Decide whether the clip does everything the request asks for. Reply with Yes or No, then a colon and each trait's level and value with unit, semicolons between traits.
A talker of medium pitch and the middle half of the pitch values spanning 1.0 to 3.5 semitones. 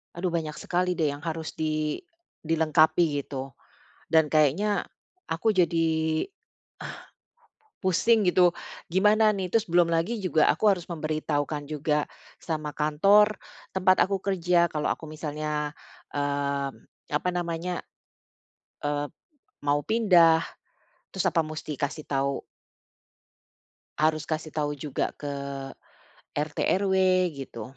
Yes: medium, 160 Hz; average, 3.2 semitones